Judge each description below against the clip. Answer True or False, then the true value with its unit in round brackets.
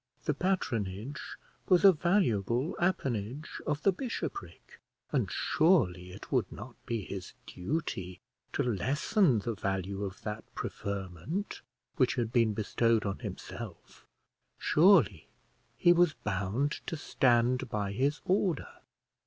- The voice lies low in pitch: True (120 Hz)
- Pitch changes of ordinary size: False (7.8 semitones)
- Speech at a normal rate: False (120 wpm)